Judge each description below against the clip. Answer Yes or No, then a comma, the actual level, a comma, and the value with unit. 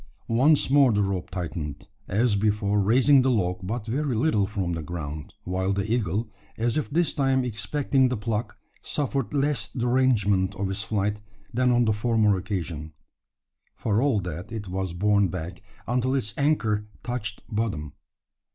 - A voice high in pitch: No, low, 105 Hz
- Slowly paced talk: No, average, 160 wpm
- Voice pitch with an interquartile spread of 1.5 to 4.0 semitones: No, average, 4.6 semitones